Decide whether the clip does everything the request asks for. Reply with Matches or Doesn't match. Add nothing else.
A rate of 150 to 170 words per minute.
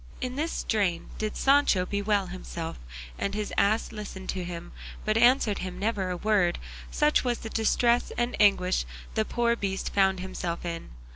Matches